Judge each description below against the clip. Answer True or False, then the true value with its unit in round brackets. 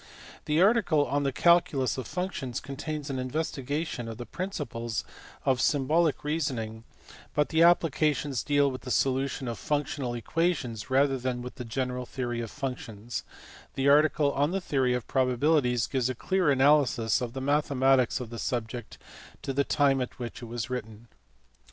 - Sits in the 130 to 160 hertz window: True (135 Hz)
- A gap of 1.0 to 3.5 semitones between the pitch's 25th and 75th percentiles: True (3.2 semitones)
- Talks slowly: False (165 wpm)